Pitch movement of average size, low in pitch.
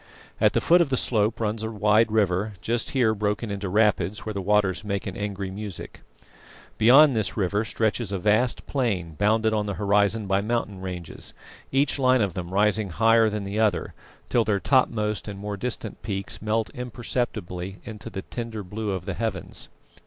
No: narrow, 2.3 semitones; low, 105 Hz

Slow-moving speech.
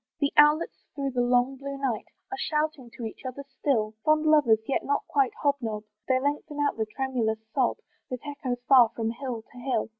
No: average, 200 wpm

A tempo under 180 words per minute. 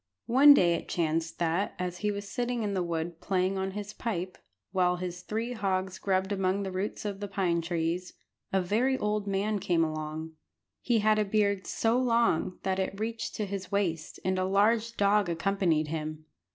No: average, 190 wpm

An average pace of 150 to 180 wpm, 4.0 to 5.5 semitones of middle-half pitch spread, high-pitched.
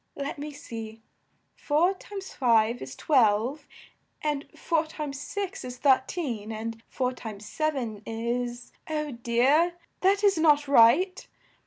No: average, 140 wpm; average, 5.1 semitones; very high, 275 Hz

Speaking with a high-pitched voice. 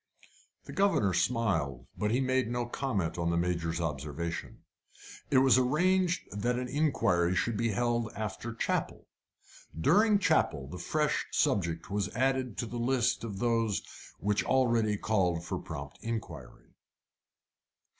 No: low, 115 Hz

